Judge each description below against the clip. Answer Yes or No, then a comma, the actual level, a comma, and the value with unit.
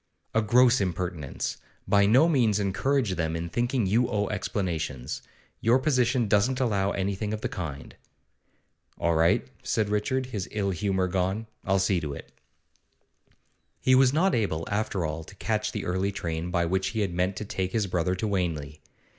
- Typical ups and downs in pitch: Yes, average, 3.9 semitones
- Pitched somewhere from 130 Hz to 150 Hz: No, low, 100 Hz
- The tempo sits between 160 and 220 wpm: Yes, average, 170 wpm